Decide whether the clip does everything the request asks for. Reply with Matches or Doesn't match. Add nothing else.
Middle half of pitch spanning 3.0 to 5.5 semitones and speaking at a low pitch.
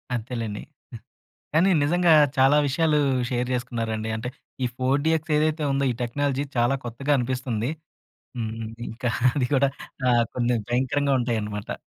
Matches